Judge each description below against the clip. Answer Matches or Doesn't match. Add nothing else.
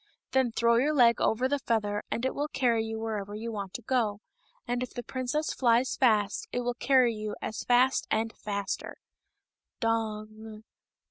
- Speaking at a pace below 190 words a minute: Matches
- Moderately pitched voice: Doesn't match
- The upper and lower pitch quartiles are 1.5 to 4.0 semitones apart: Matches